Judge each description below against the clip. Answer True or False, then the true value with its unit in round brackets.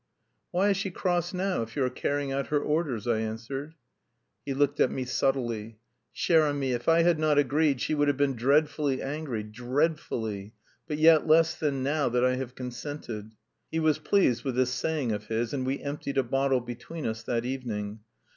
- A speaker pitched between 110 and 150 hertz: True (135 Hz)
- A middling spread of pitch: True (4.1 semitones)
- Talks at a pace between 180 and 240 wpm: True (200 wpm)